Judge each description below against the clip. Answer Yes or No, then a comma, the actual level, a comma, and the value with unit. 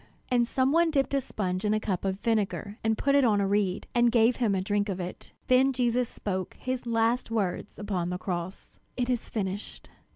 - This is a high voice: Yes, high, 220 Hz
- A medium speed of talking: No, fast, 215 wpm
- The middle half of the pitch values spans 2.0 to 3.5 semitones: No, average, 4.2 semitones